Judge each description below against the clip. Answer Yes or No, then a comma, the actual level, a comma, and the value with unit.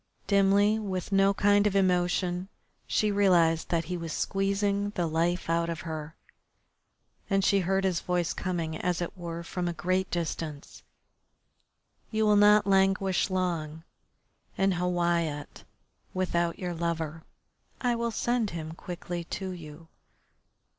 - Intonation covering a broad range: No, average, 2.7 semitones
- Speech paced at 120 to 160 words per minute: Yes, slow, 135 wpm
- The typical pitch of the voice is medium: Yes, medium, 180 Hz